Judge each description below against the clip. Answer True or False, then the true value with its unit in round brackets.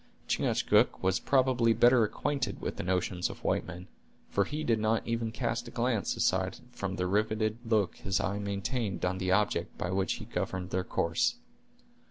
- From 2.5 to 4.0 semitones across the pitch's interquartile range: True (3.7 semitones)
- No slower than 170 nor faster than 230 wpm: True (180 wpm)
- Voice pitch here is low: True (105 Hz)